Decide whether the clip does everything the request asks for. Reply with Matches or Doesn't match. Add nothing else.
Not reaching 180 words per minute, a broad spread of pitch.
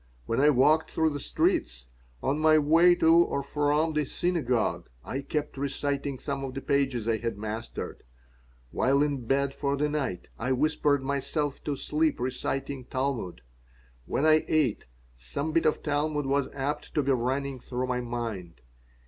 Doesn't match